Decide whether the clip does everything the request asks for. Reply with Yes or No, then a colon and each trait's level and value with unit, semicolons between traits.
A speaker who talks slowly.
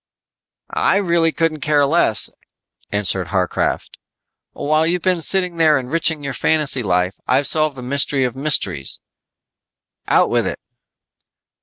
Yes: slow, 130 wpm